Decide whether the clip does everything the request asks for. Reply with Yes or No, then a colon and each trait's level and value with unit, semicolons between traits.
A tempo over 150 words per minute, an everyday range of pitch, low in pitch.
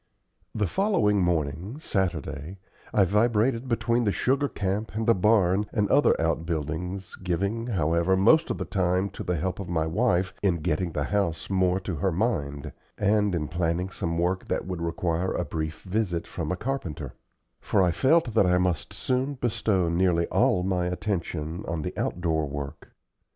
Yes: average, 170 wpm; average, 4.0 semitones; very low, 90 Hz